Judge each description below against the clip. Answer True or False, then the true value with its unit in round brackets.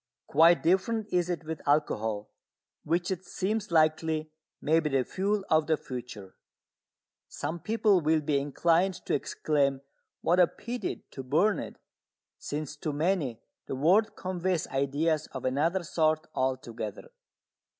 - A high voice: False (160 Hz)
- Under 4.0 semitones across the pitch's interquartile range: False (4.3 semitones)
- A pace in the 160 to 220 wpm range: False (140 wpm)